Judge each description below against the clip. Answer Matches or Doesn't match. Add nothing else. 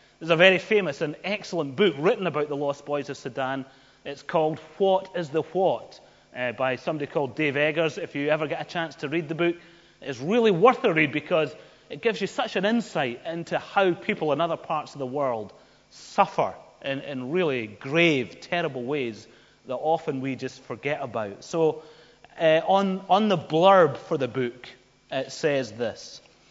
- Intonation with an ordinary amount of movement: Matches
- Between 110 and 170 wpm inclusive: Doesn't match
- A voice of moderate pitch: Matches